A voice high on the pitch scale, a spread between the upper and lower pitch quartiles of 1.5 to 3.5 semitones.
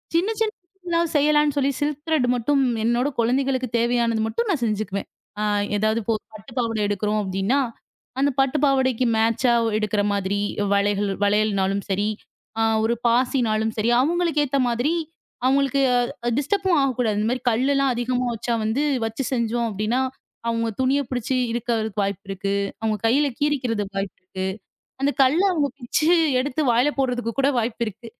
No: high, 240 Hz; average, 4.2 semitones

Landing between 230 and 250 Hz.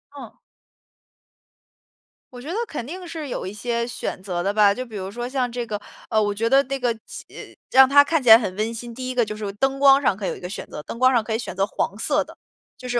Yes: high, 240 Hz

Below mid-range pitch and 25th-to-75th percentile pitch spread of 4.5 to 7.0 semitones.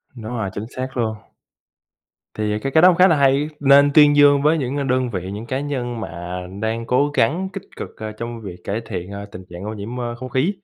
Yes: low, 125 Hz; average, 4.9 semitones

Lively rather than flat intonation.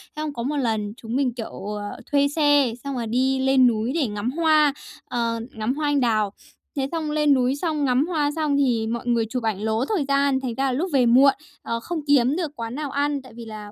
No: average, 3.8 semitones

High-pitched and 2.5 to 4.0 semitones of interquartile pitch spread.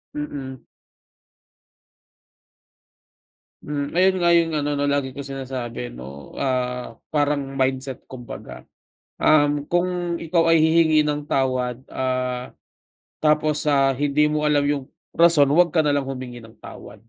No: medium, 145 Hz; average, 2.8 semitones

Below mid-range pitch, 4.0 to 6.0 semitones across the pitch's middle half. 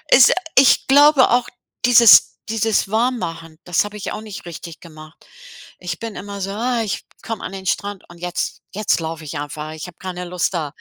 No: high, 190 Hz; average, 5.1 semitones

